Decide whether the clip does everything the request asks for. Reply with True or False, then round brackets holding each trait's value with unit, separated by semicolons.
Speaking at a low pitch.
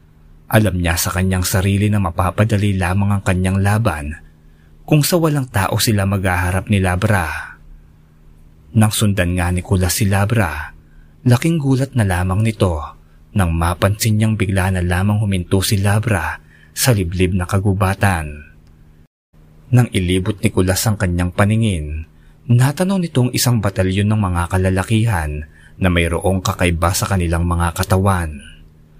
True (95 Hz)